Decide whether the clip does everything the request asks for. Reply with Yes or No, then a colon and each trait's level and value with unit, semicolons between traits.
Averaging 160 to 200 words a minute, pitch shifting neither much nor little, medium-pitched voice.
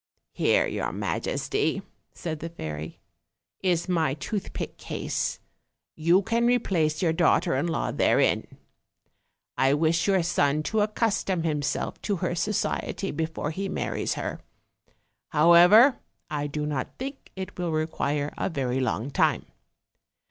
No: slow, 135 wpm; average, 4.3 semitones; medium, 165 Hz